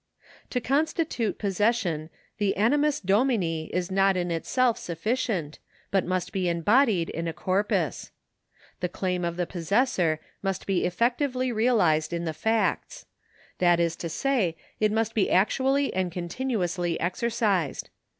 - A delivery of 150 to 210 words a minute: No, slow, 135 wpm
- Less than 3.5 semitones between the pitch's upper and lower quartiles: No, average, 5.2 semitones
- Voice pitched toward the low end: No, high, 195 Hz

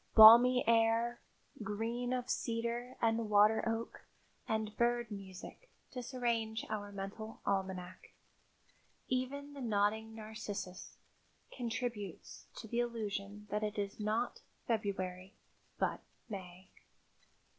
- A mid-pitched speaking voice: No, high, 220 Hz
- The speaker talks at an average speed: No, slow, 100 wpm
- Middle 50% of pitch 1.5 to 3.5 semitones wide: Yes, average, 2.7 semitones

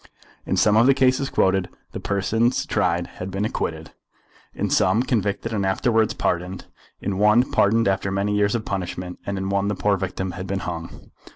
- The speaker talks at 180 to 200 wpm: Yes, average, 185 wpm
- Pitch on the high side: No, low, 100 Hz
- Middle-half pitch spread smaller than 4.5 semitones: Yes, narrow, 2.5 semitones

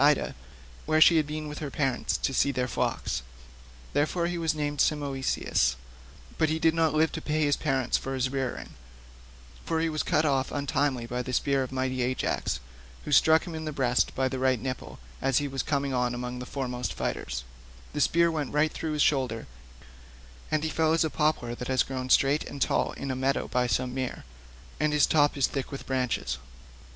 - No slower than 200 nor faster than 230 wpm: Yes, fast, 205 wpm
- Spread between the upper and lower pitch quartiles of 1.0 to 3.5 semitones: Yes, average, 3.0 semitones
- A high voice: No, medium, 140 Hz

